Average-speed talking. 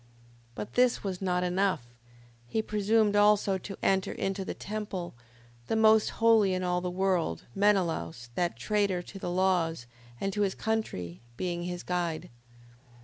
Yes: average, 155 wpm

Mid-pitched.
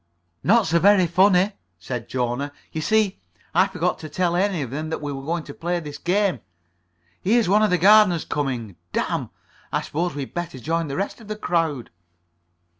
Yes: medium, 170 Hz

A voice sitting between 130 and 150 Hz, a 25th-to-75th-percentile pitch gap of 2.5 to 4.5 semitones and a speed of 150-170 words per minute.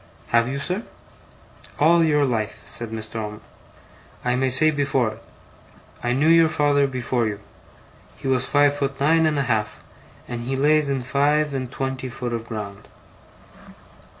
Yes: low, 135 Hz; average, 3.5 semitones; average, 165 wpm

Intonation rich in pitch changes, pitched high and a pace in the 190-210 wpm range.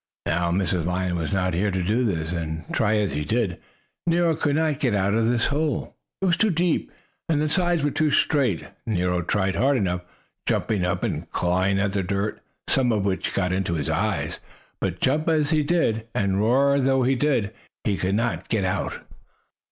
No: wide, 7.3 semitones; low, 105 Hz; average, 200 wpm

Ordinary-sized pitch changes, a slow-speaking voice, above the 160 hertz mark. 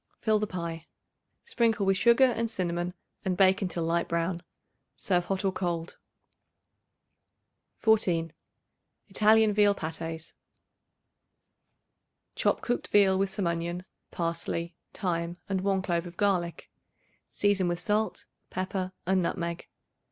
Yes: average, 3.1 semitones; slow, 120 wpm; medium, 185 Hz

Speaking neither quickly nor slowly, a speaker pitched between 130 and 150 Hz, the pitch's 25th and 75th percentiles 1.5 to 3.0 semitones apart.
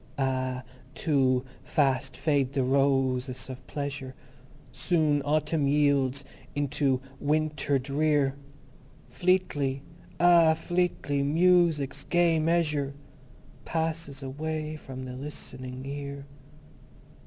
No: slow, 110 wpm; medium, 140 Hz; narrow, 2.6 semitones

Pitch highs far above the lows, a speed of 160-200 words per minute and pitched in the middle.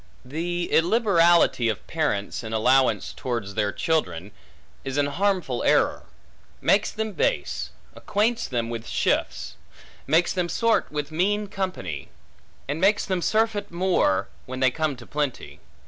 No: wide, 7.6 semitones; slow, 135 wpm; medium, 160 Hz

